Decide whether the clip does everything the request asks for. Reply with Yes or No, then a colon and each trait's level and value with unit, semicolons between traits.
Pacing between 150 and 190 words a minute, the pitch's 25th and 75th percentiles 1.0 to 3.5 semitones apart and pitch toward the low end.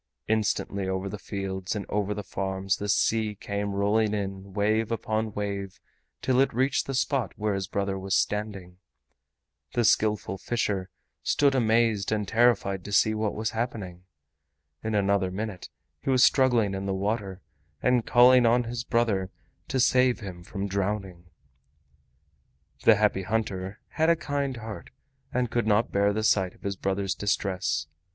Yes: average, 160 wpm; average, 2.8 semitones; low, 105 Hz